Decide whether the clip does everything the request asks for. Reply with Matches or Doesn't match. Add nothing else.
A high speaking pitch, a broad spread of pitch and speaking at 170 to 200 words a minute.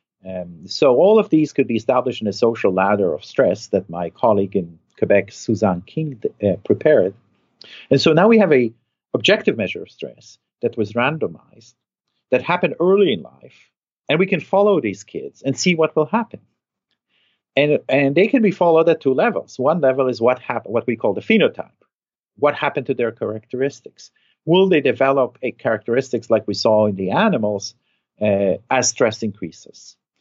Doesn't match